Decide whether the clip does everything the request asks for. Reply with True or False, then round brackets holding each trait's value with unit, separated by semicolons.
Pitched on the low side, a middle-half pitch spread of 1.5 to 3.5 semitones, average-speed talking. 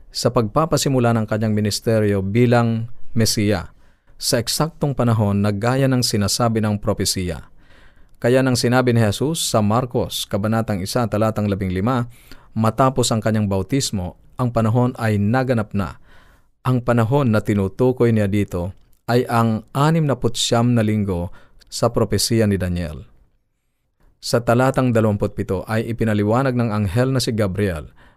True (115 Hz; 3.2 semitones; 135 wpm)